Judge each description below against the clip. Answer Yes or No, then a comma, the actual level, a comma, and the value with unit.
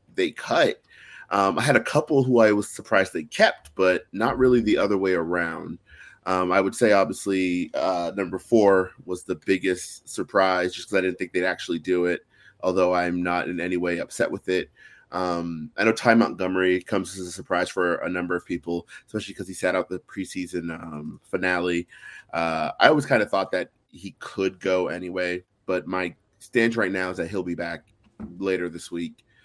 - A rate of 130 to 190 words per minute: No, average, 200 wpm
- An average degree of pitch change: No, narrow, 1.8 semitones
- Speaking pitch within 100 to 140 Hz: No, very low, 90 Hz